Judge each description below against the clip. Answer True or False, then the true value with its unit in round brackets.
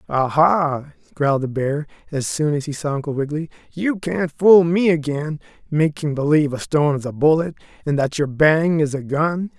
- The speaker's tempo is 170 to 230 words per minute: True (195 wpm)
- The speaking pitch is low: False (150 Hz)